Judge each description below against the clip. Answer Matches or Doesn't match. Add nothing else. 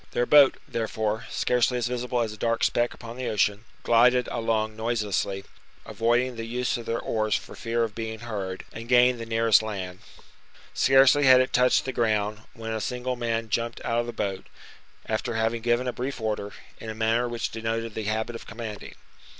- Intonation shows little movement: Matches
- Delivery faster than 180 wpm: Matches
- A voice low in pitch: Matches